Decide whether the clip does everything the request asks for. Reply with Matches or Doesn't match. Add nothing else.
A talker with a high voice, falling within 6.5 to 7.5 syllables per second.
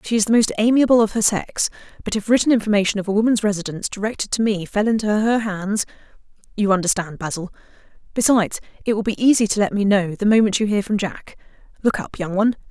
Matches